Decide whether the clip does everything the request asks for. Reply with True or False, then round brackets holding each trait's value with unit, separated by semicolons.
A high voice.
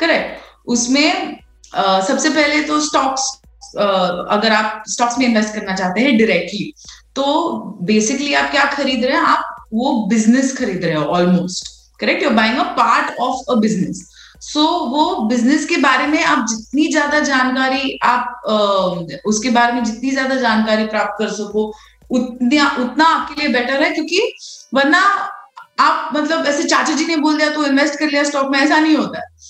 True (265 Hz)